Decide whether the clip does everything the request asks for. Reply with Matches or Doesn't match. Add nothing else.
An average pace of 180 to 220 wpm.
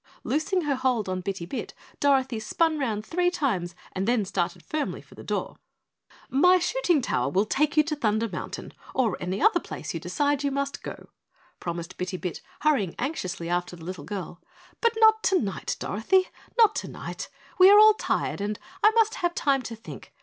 Matches